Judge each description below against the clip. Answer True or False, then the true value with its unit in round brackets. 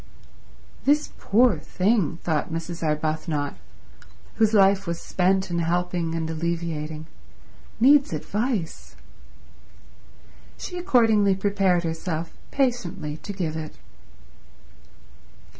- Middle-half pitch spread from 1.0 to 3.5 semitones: False (4.3 semitones)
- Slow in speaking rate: True (90 wpm)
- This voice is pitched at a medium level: True (175 Hz)